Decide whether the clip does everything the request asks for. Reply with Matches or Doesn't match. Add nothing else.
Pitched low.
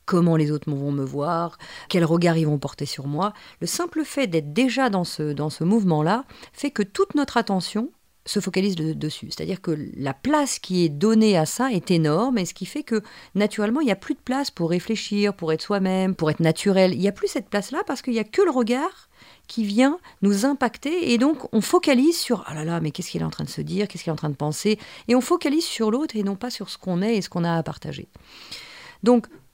Doesn't match